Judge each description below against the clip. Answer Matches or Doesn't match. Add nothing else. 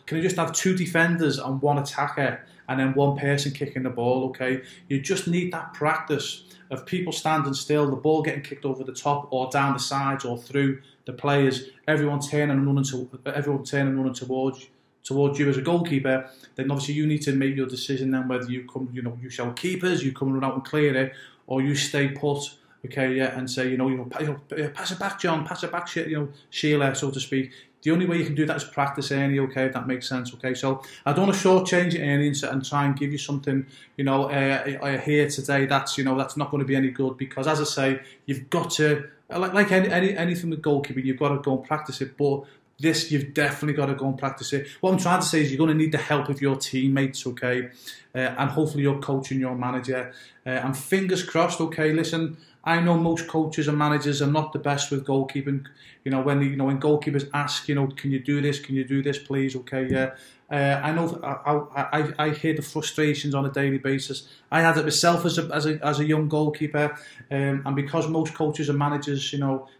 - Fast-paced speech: Matches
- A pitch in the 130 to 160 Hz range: Matches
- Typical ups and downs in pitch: Doesn't match